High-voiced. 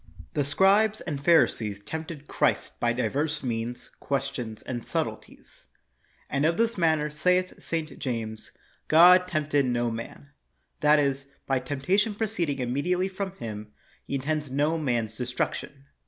No: medium, 145 Hz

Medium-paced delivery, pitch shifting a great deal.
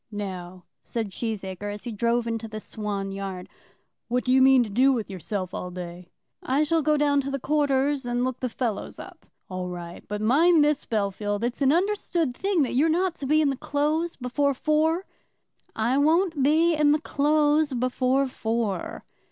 Yes: average, 185 wpm; wide, 6.1 semitones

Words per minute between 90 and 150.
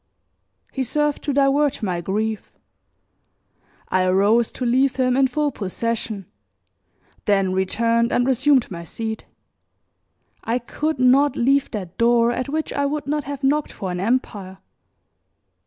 Yes: average, 140 wpm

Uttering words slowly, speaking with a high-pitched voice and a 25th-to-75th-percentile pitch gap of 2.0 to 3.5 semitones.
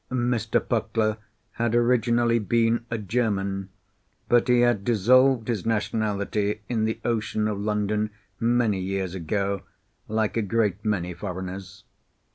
No: slow, 125 wpm; low, 110 Hz; average, 2.8 semitones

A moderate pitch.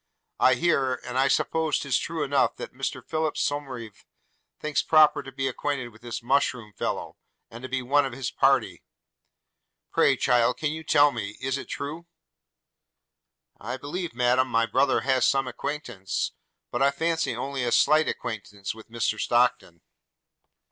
No: low, 130 Hz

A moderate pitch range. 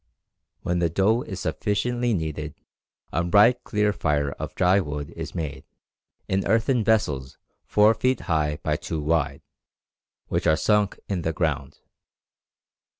No: wide, 5.8 semitones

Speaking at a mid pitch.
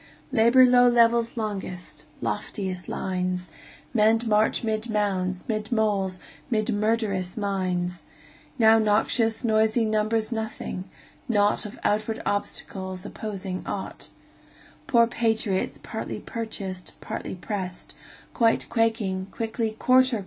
No: high, 215 Hz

